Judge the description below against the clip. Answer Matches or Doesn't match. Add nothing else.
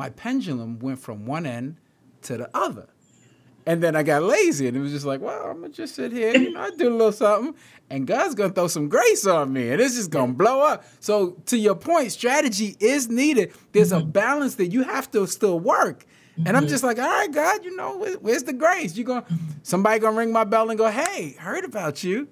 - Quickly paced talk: Matches